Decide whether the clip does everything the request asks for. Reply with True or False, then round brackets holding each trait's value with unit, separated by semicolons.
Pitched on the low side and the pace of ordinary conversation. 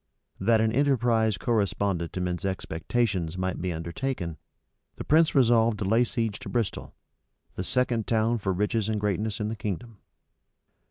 True (110 Hz; 155 wpm)